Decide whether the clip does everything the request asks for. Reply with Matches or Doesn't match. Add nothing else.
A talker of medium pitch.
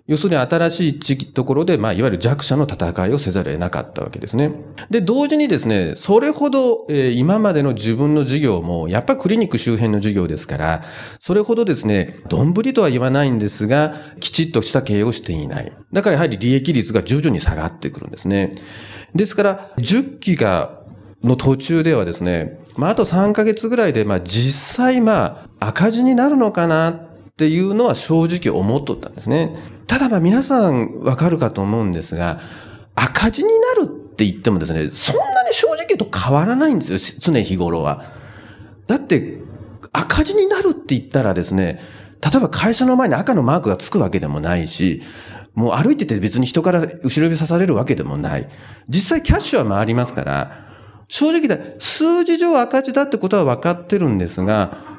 Matches